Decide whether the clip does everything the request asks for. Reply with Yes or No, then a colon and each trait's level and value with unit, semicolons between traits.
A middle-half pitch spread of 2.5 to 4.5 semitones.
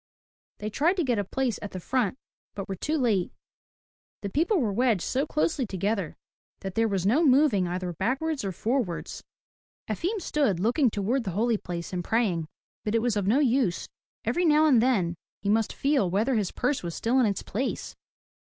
No: wide, 5.6 semitones